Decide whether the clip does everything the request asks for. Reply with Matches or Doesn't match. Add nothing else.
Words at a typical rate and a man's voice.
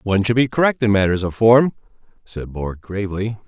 Matches